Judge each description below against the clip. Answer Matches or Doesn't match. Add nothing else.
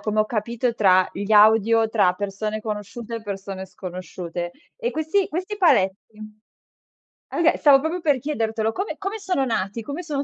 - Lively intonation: Matches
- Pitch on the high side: Matches